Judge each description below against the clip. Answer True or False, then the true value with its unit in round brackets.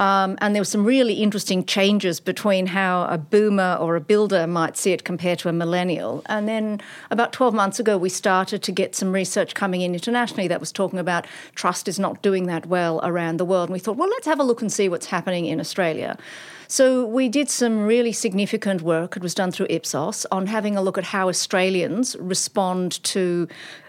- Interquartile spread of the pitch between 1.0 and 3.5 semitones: True (2.9 semitones)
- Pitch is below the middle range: False (190 Hz)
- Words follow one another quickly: True (215 wpm)